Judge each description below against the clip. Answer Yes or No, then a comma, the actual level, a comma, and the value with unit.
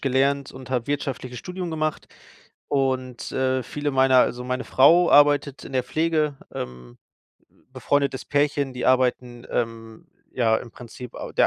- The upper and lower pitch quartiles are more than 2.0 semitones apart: Yes, narrow, 2.5 semitones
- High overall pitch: No, low, 130 Hz